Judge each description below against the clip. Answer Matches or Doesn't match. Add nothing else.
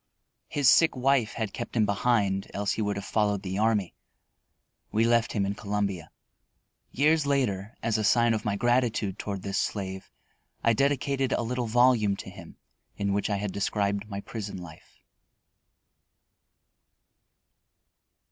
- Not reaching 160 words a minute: Matches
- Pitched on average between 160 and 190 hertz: Doesn't match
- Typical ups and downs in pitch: Matches